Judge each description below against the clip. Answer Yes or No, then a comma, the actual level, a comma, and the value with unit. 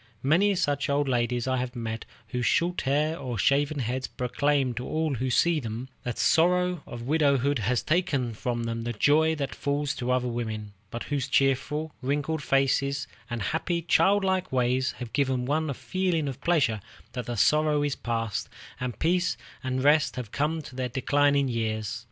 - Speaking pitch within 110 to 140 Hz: Yes, low, 135 Hz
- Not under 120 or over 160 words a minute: No, average, 180 wpm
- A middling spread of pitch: Yes, average, 3.9 semitones